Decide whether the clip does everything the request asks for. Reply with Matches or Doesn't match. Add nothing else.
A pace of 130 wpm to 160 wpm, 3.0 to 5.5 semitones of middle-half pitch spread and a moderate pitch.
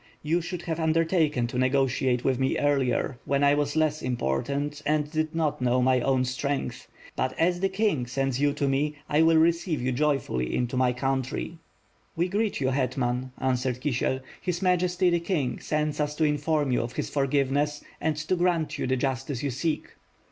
Doesn't match